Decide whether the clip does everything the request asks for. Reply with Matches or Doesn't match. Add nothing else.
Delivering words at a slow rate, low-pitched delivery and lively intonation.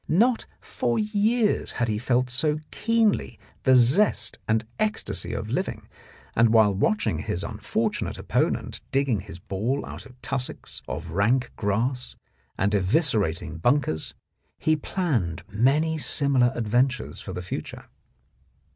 Matches